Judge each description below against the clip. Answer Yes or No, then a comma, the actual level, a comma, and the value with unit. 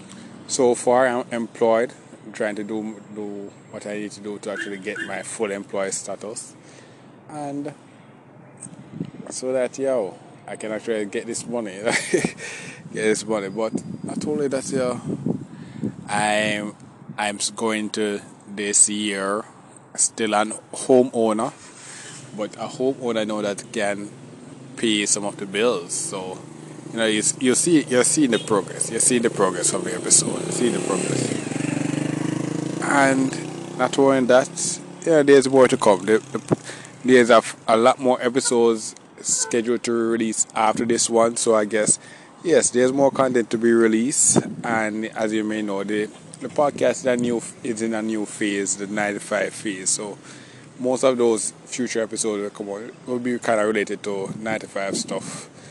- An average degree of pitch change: Yes, average, 3.4 semitones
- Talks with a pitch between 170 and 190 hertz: No, low, 115 Hz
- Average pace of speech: Yes, average, 160 wpm